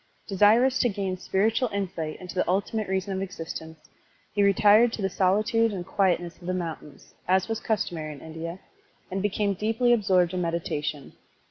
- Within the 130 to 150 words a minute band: No, average, 165 wpm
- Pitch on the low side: No, high, 190 Hz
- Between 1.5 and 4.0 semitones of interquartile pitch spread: Yes, average, 3.3 semitones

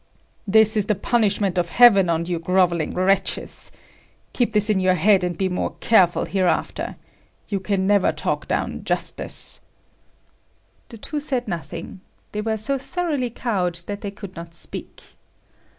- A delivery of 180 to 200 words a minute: No, average, 150 wpm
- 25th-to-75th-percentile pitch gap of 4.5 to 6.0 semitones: No, average, 3.3 semitones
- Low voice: No, high, 200 Hz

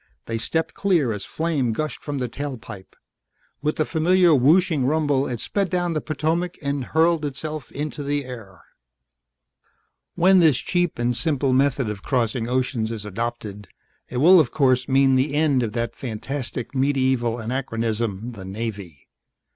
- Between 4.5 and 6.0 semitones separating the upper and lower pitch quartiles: Yes, average, 4.8 semitones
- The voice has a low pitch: Yes, low, 130 Hz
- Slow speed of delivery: No, average, 155 wpm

